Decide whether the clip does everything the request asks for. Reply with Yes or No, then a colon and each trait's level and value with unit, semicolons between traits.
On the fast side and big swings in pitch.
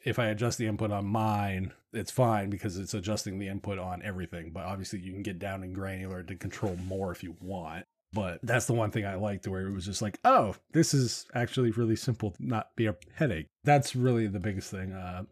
No: fast, 230 wpm; average, 3.1 semitones